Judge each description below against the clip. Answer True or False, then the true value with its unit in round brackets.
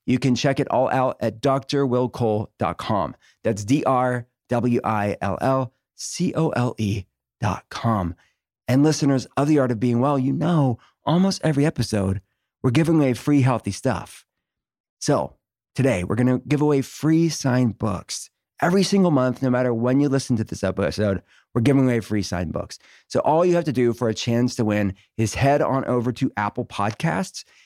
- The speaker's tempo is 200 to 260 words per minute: False (165 wpm)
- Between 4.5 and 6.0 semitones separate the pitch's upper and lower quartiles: False (4.1 semitones)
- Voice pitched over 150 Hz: False (125 Hz)